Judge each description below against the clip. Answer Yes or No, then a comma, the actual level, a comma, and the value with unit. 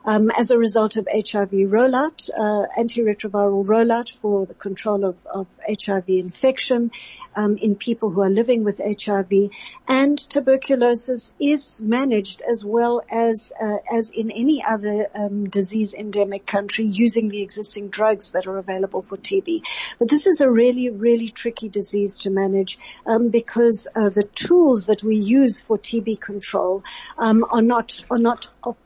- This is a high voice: Yes, high, 220 Hz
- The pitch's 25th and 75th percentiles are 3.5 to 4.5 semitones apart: No, average, 2.8 semitones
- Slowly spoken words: No, average, 160 wpm